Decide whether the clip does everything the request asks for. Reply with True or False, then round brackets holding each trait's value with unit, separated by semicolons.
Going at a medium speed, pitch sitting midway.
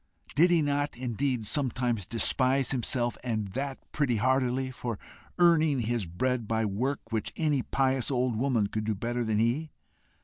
False (160 wpm; 125 Hz)